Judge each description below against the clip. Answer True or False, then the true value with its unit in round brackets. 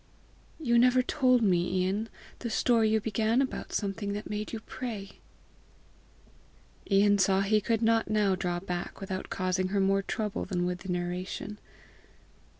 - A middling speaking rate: True (150 wpm)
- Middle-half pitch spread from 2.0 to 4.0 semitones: True (3.1 semitones)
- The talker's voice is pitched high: True (205 Hz)